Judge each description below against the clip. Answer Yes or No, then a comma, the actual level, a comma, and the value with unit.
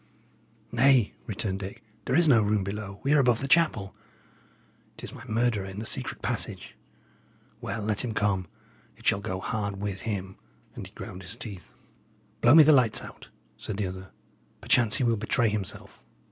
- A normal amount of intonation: Yes, average, 3.6 semitones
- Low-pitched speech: Yes, low, 105 Hz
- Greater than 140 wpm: Yes, average, 180 wpm